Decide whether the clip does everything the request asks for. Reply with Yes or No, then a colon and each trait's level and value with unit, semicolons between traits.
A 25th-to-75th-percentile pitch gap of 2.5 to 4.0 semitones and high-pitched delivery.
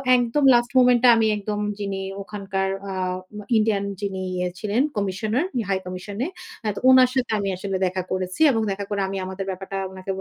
Yes: average, 3.0 semitones; high, 200 Hz